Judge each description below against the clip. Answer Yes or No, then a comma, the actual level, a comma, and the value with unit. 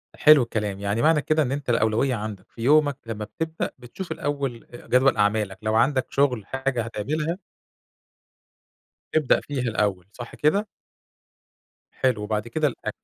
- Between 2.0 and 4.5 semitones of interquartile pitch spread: No, average, 5.0 semitones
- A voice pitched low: Yes, low, 125 Hz